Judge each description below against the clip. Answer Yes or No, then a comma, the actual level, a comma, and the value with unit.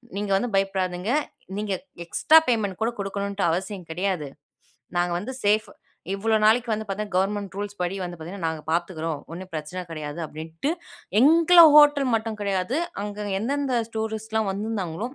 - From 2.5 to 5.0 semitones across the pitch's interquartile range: Yes, average, 3.6 semitones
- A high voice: Yes, high, 200 Hz